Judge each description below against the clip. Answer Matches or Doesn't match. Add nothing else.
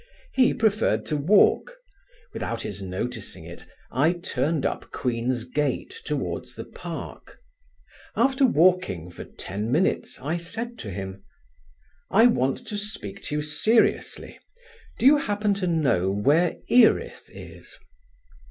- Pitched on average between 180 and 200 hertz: Doesn't match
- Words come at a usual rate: Doesn't match